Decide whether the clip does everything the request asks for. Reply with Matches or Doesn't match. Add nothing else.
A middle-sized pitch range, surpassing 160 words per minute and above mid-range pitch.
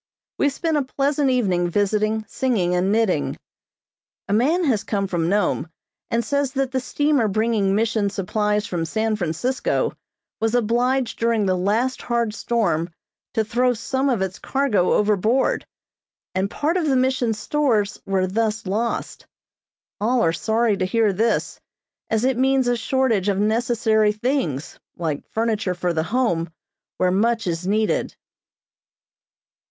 Doesn't match